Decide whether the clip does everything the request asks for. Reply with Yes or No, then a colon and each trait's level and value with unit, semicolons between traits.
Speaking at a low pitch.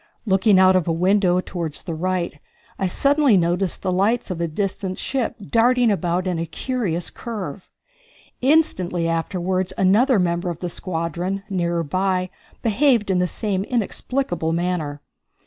No: medium, 185 Hz